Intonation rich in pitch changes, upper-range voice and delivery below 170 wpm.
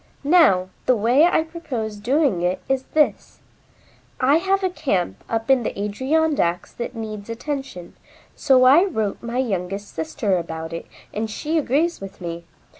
Yes: wide, 6.9 semitones; high, 235 Hz; average, 155 wpm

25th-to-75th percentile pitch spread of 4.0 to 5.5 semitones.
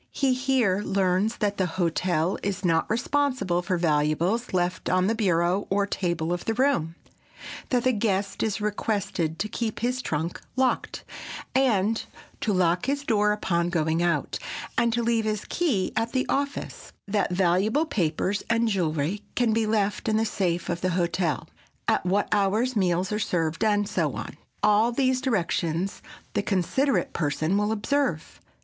Yes: average, 4.4 semitones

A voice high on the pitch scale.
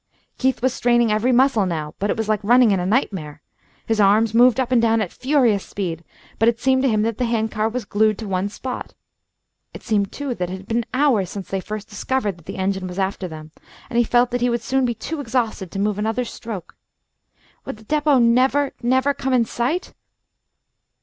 Yes: high, 225 Hz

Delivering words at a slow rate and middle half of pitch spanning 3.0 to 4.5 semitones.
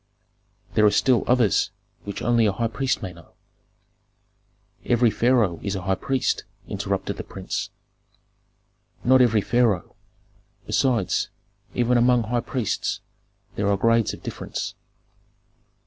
Yes: slow, 125 wpm; average, 3.3 semitones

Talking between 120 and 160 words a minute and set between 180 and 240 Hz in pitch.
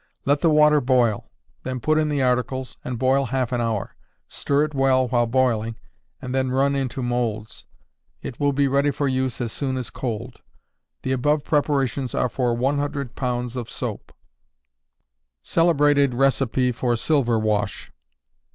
No: average, 155 wpm; low, 130 Hz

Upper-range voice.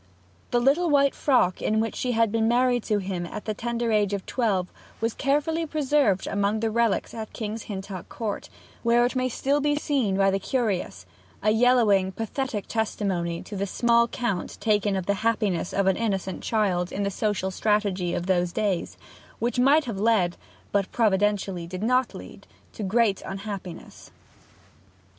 Yes: high, 215 Hz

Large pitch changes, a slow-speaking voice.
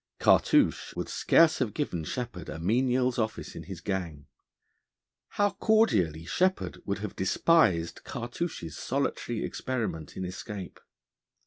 Yes: wide, 6.8 semitones; slow, 120 wpm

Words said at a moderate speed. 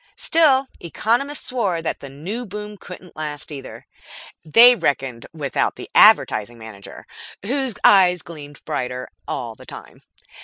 No: slow, 130 wpm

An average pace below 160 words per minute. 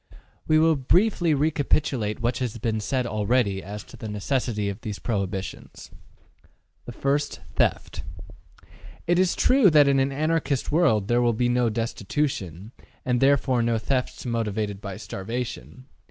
Yes: average, 140 wpm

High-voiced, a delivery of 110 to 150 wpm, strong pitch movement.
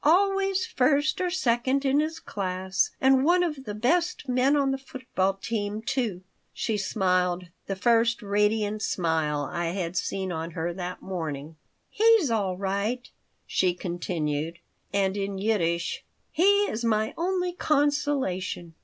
Yes: high, 210 Hz; average, 140 wpm; wide, 7.3 semitones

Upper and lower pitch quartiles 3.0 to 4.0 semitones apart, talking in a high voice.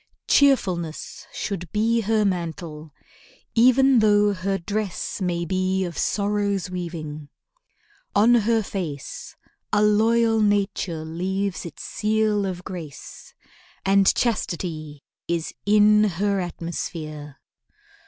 Yes: average, 3.7 semitones; high, 195 Hz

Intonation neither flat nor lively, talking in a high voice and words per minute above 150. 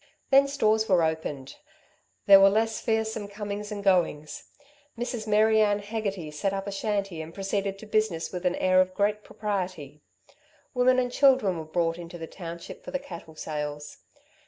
Yes: average, 4.3 semitones; high, 195 Hz; average, 170 wpm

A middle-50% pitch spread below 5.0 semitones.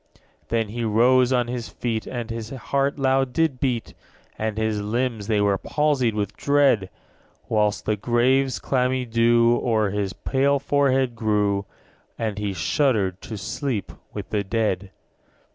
Yes: average, 3.7 semitones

